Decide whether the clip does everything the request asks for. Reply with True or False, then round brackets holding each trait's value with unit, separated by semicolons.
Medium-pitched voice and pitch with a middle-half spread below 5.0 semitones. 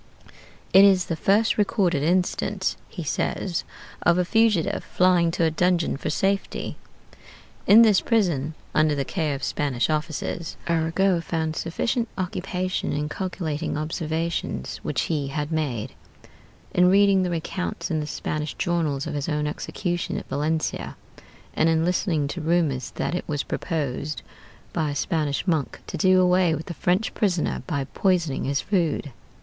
True (165 Hz; 3.4 semitones)